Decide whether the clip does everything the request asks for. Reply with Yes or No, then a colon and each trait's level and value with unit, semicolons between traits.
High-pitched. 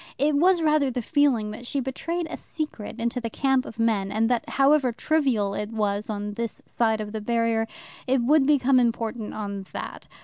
Yes: high, 235 Hz